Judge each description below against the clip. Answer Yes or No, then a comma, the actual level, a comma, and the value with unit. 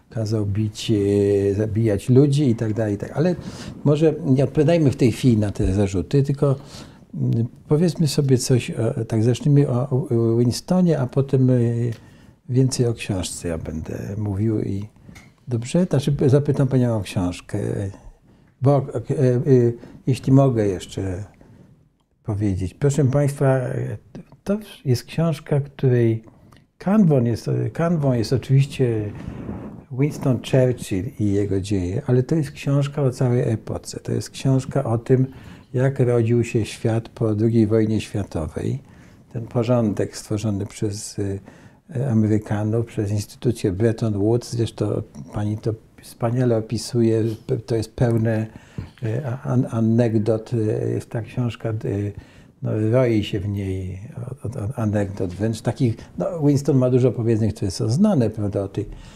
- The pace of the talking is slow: No, average, 125 wpm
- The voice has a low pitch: Yes, low, 120 Hz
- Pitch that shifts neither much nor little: Yes, average, 3.7 semitones